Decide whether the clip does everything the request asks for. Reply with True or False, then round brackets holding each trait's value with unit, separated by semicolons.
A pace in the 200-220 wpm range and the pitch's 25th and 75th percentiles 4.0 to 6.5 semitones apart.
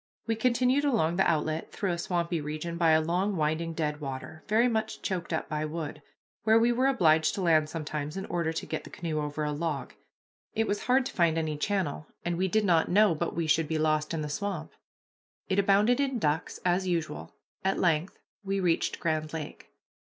True (205 wpm; 4.3 semitones)